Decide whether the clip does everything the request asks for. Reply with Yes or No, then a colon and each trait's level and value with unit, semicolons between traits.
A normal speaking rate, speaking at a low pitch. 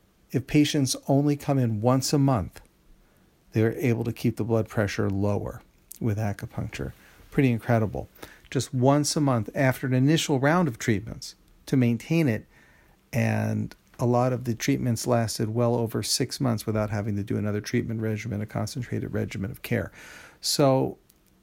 Yes: average, 160 wpm; low, 115 Hz